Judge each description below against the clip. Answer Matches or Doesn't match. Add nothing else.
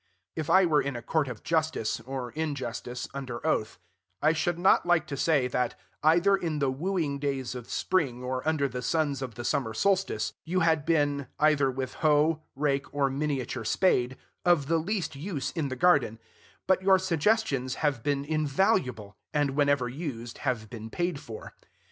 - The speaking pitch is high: Doesn't match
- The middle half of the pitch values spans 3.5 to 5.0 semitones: Matches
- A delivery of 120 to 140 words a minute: Doesn't match